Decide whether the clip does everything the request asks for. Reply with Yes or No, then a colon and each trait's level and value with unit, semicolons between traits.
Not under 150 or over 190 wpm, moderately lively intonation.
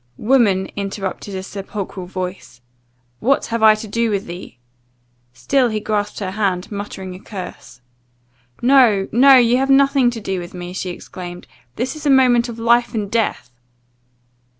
Yes: average, 160 wpm; average, 4.2 semitones